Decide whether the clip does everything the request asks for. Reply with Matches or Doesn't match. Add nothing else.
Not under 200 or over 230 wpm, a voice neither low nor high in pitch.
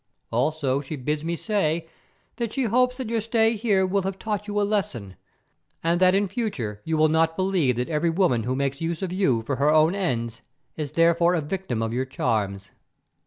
Matches